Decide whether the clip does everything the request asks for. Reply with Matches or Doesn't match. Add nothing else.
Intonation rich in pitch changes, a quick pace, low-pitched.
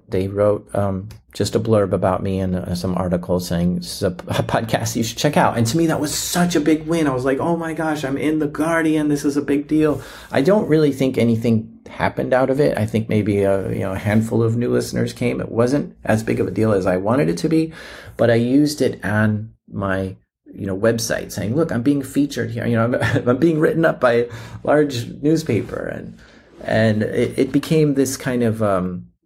Matches